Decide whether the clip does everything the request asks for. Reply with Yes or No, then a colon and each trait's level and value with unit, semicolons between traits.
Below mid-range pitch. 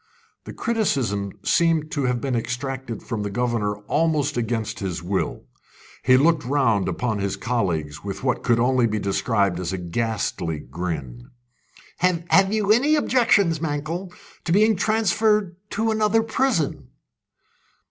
Yes: low, 125 Hz